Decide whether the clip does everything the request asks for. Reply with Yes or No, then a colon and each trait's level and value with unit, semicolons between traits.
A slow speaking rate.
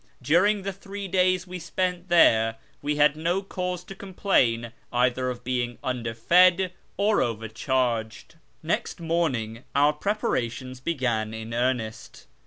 Yes: slow, 125 wpm